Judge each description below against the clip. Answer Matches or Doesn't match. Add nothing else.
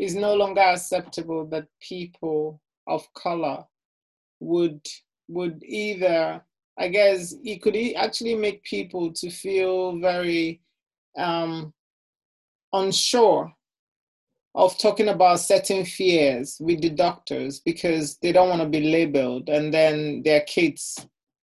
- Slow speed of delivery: Matches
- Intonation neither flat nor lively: Matches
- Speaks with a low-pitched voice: Doesn't match